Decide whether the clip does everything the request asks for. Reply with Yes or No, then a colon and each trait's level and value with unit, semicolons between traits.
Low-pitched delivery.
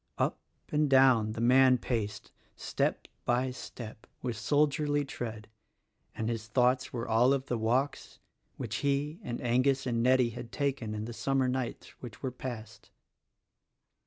Yes: low, 125 Hz